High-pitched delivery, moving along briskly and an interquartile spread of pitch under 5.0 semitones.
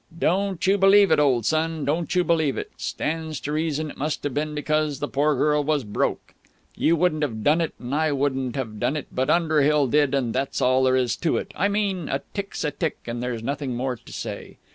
No: medium, 150 Hz; fast, 230 wpm; average, 3.4 semitones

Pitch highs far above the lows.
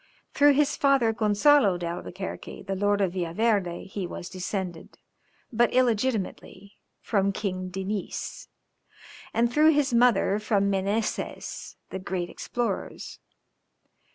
No: average, 3.9 semitones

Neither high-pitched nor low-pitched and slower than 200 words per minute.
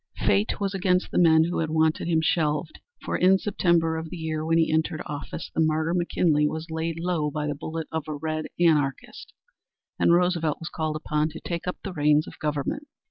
No: medium, 160 Hz; fast, 205 wpm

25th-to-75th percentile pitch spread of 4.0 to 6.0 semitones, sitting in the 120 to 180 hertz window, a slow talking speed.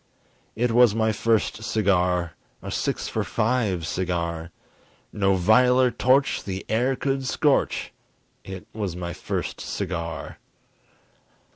No: wide, 5.4 semitones; low, 105 Hz; slow, 115 wpm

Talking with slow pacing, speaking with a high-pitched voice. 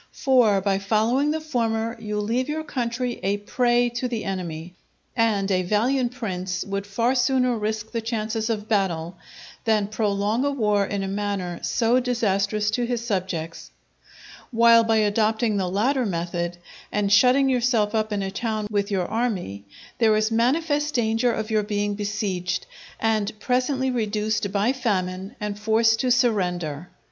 No: average, 155 wpm; high, 215 Hz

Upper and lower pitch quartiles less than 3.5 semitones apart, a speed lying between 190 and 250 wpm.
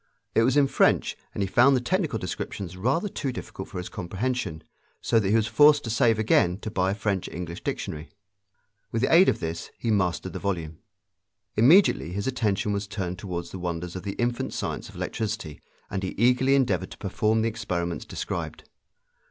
No: average, 5.0 semitones; average, 195 wpm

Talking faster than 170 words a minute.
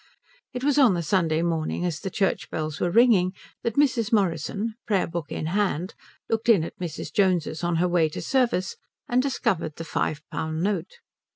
Yes: average, 185 wpm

